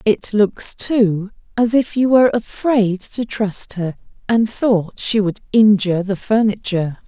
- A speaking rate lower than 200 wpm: Yes, average, 155 wpm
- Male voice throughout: No, female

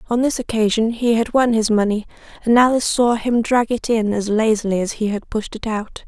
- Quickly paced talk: Yes, fast, 225 wpm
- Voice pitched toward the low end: No, high, 225 Hz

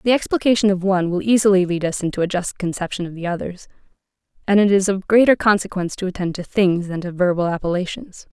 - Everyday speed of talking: No, fast, 210 wpm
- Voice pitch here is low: No, high, 190 Hz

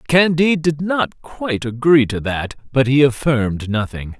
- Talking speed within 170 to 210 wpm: No, average, 155 wpm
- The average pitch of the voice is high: No, low, 135 Hz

